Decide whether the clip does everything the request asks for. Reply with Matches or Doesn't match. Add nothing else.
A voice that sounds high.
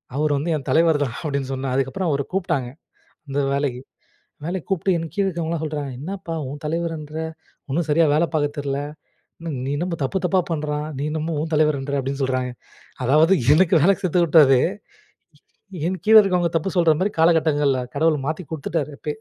Doesn't match